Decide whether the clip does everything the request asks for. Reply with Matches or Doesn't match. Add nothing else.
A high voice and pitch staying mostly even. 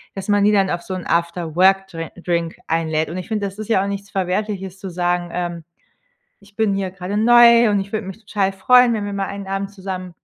Matches